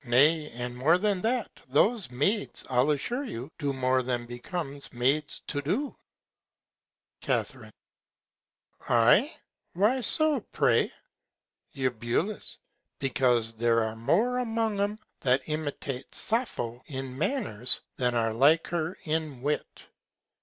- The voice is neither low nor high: Yes, medium, 145 Hz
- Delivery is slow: Yes, slow, 120 wpm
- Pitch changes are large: Yes, wide, 8.1 semitones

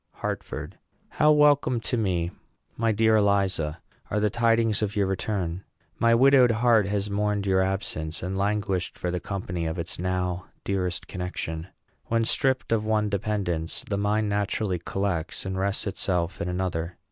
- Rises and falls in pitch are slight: No, average, 3.2 semitones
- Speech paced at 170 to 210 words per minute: No, average, 160 wpm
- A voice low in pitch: Yes, low, 100 Hz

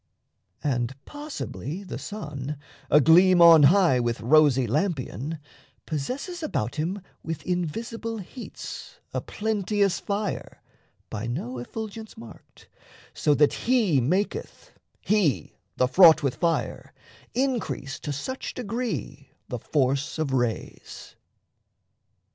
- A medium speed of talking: No, slow, 105 wpm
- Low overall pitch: No, medium, 165 Hz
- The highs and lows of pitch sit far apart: Yes, wide, 7.5 semitones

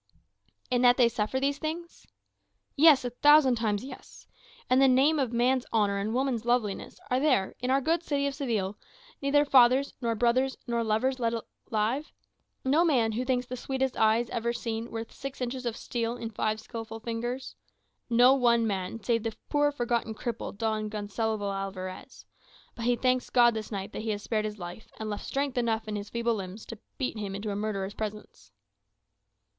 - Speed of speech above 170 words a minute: Yes, average, 185 wpm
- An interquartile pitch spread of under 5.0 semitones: Yes, average, 3.2 semitones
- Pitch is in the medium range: No, high, 235 Hz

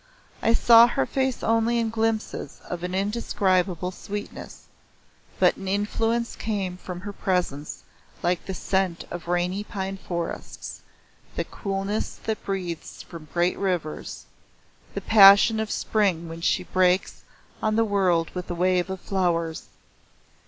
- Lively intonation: No, average, 3.1 semitones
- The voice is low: No, high, 190 Hz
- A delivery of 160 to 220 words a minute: No, average, 140 wpm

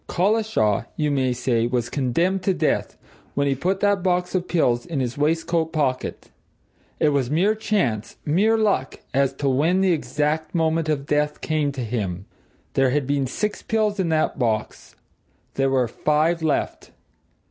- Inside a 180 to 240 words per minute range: No, average, 165 wpm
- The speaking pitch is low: No, medium, 150 Hz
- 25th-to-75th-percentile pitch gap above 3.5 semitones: Yes, average, 5.3 semitones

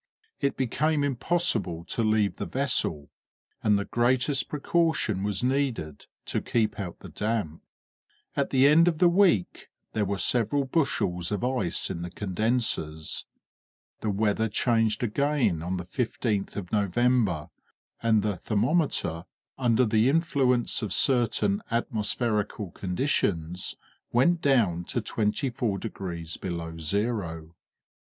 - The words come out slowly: Yes, slow, 125 wpm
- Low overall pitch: Yes, low, 110 Hz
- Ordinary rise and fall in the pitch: No, wide, 5.8 semitones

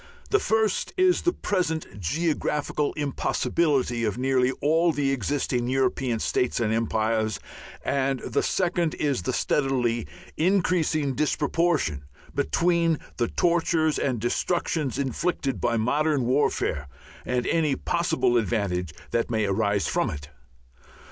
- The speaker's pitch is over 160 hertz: No, low, 135 Hz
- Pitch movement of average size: No, wide, 5.7 semitones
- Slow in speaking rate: Yes, slow, 120 wpm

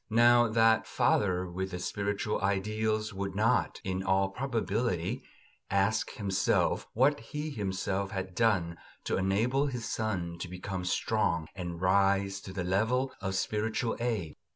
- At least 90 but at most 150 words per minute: Yes, average, 140 wpm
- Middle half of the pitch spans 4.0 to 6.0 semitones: No, average, 3.1 semitones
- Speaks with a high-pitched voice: No, low, 100 Hz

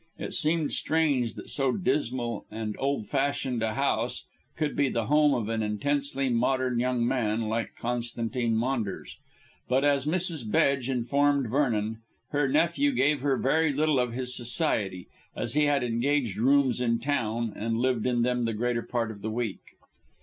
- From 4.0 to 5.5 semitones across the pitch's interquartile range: No, average, 3.6 semitones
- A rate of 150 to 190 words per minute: Yes, average, 165 wpm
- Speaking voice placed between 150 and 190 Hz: No, low, 125 Hz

